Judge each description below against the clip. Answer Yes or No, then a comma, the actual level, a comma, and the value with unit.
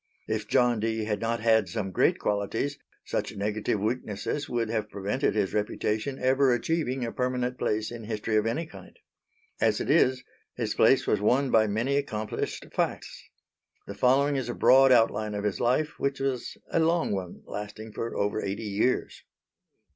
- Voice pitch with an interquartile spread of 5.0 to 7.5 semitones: No, average, 3.5 semitones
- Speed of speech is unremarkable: Yes, average, 170 wpm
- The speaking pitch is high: No, low, 115 Hz